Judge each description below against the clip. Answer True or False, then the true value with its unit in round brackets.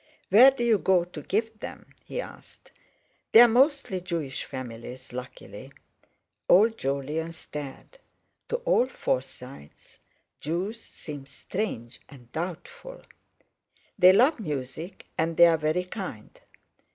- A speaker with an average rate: False (115 wpm)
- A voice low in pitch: False (170 Hz)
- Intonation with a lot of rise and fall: True (8.4 semitones)